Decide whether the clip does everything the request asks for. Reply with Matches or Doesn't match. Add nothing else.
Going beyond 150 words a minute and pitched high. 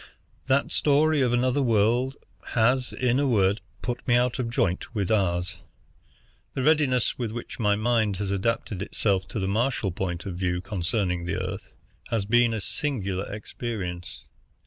Doesn't match